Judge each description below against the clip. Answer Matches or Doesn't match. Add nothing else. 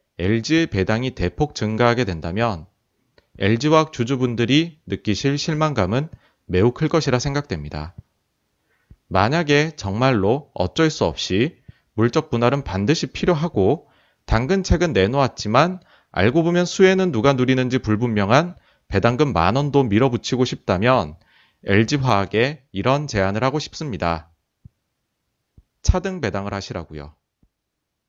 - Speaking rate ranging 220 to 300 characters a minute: Matches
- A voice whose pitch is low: Matches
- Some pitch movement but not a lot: Doesn't match